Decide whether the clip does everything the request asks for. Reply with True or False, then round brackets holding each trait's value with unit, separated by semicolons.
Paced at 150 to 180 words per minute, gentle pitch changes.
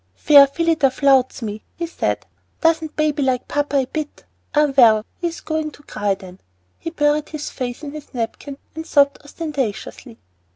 False (170 wpm; 3.2 semitones)